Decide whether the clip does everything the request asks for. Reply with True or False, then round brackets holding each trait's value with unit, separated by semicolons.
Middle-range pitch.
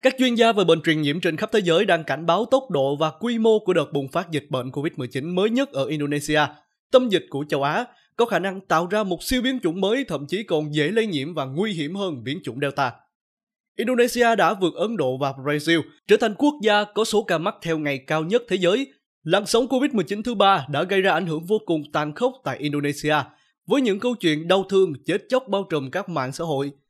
True (170 Hz)